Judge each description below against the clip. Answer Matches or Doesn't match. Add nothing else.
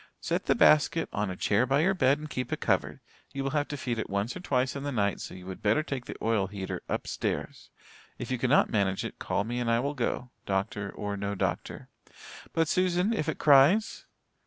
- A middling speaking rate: Doesn't match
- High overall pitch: Doesn't match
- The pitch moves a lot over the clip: Matches